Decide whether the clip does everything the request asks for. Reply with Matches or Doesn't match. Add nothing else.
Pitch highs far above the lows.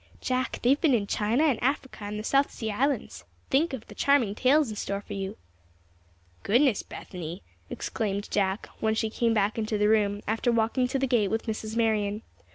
Doesn't match